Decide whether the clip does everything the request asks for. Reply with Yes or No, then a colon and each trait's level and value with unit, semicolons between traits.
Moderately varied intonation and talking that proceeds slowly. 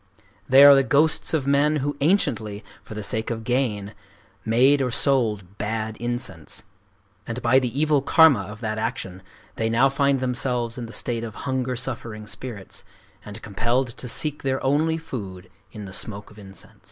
No: average, 4.0 semitones; average, 175 wpm